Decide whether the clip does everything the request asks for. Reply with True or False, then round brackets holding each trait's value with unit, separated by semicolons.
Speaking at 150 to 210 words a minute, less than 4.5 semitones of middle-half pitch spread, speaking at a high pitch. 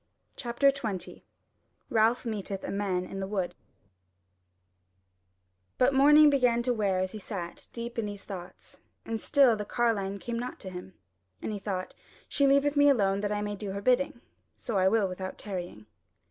True (175 wpm; 4.1 semitones; 210 Hz)